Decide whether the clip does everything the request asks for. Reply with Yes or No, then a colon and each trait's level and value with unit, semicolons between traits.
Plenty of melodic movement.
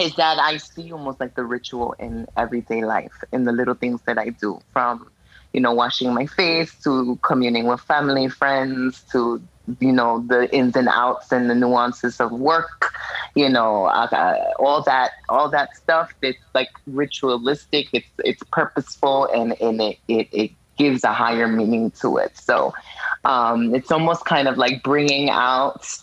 No: average, 2.8 semitones